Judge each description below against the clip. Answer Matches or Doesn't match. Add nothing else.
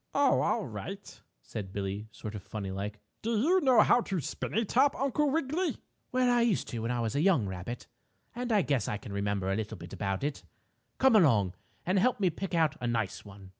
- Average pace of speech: Doesn't match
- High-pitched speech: Doesn't match